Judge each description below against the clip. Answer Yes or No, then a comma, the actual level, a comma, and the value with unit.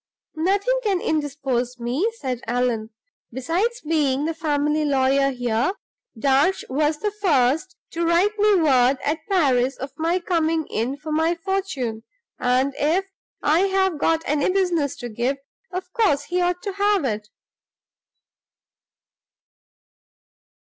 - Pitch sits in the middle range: No, very high, 305 Hz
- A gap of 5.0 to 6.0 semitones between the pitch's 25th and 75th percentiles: Yes, wide, 5.6 semitones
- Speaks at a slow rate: Yes, slow, 130 wpm